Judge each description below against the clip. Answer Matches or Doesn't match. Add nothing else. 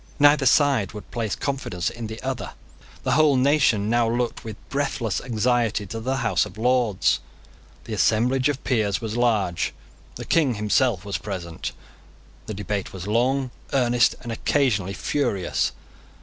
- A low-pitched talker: Matches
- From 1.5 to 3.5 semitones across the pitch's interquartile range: Doesn't match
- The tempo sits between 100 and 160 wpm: Matches